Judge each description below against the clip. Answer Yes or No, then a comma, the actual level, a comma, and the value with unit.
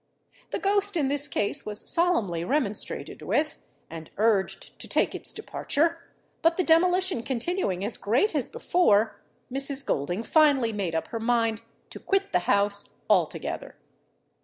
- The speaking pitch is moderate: No, very high, 255 Hz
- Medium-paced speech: Yes, average, 145 wpm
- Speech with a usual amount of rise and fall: No, wide, 8.3 semitones